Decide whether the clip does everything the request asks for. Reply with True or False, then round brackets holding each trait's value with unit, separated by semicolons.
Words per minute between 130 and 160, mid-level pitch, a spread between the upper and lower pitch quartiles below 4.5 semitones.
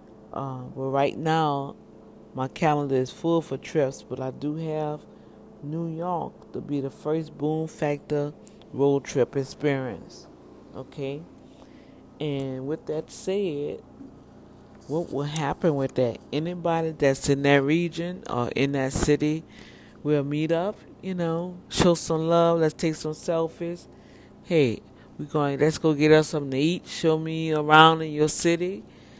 True (150 wpm; 150 Hz; 2.9 semitones)